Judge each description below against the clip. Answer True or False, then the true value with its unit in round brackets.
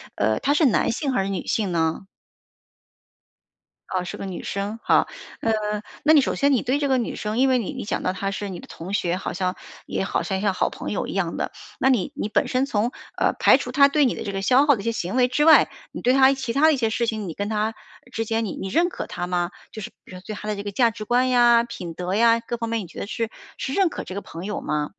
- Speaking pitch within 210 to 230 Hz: True (220 Hz)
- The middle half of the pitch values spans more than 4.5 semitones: True (4.9 semitones)